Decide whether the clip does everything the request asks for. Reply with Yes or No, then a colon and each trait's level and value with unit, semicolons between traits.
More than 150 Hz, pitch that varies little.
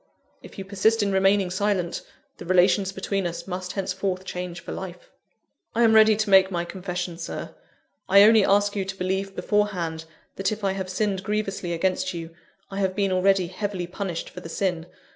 Yes: high, 190 Hz; narrow, 1.8 semitones